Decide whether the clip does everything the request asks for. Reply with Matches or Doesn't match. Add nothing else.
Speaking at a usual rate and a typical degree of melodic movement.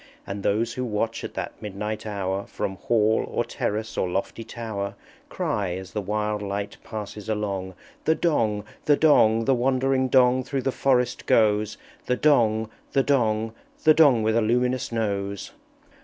Matches